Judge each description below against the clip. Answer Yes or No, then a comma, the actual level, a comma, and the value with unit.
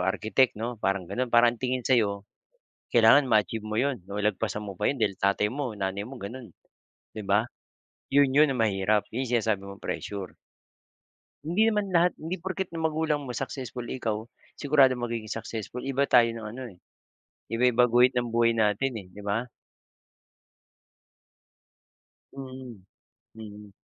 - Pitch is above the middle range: No, low, 115 Hz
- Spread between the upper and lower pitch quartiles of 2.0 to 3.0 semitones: No, average, 4.0 semitones